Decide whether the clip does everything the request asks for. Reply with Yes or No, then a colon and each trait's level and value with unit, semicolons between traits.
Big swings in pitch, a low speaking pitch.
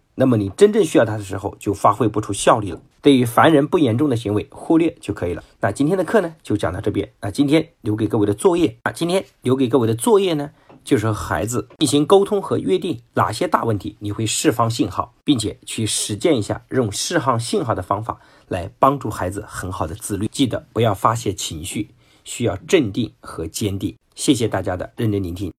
Yes: wide, 5.8 semitones; low, 115 Hz